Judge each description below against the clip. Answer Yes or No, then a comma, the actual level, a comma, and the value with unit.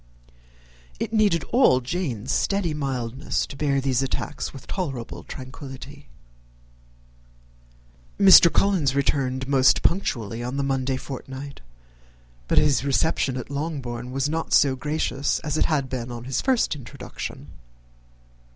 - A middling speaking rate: No, slow, 130 wpm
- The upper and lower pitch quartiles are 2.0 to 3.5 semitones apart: Yes, average, 2.9 semitones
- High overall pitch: No, low, 135 Hz